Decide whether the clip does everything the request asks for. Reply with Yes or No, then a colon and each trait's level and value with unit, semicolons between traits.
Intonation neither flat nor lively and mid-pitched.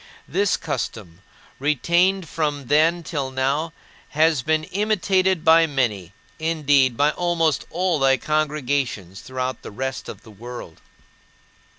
Yes: average, 4.1 semitones; medium, 150 Hz